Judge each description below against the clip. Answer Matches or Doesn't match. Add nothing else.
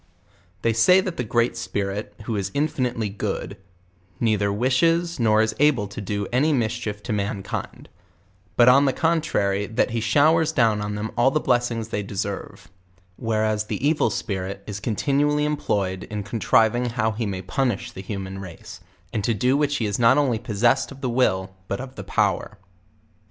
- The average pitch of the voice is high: Doesn't match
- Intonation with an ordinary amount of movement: Matches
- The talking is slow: Doesn't match